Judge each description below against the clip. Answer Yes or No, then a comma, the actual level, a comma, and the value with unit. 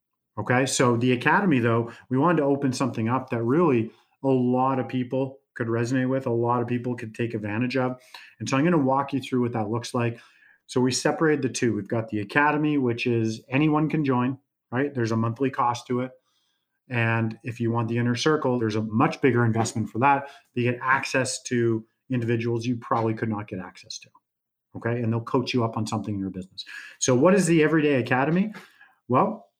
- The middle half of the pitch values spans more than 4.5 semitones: No, average, 2.7 semitones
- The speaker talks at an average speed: No, fast, 215 wpm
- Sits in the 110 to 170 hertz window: Yes, low, 125 Hz